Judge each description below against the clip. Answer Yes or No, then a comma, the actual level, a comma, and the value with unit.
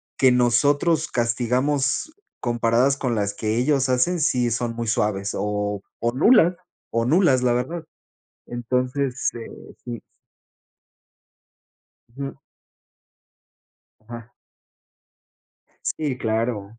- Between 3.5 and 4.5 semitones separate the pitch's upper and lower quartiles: No, average, 3.0 semitones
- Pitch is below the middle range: Yes, low, 125 Hz